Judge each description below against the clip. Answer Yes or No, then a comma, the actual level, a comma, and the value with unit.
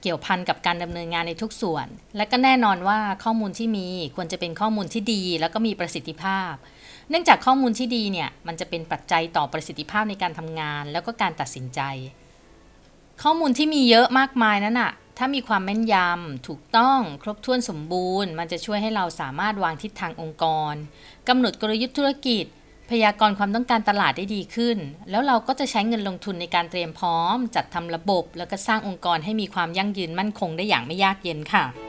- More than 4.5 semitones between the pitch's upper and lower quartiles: Yes, average, 4.9 semitones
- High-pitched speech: Yes, high, 195 Hz